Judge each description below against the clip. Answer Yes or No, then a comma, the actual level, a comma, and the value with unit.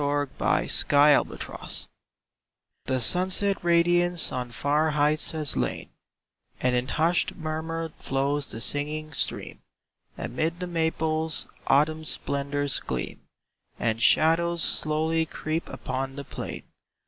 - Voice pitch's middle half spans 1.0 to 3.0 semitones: Yes, narrow, 2.6 semitones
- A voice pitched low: No, medium, 155 Hz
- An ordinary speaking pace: No, slow, 110 wpm